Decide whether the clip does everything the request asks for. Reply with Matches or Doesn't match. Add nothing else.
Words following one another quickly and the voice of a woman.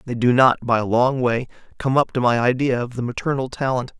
Doesn't match